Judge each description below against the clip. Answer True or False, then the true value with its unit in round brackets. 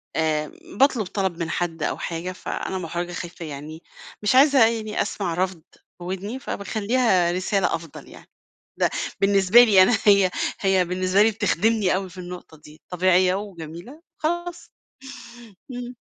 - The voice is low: False (185 Hz)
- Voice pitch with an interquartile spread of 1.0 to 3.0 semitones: False (3.7 semitones)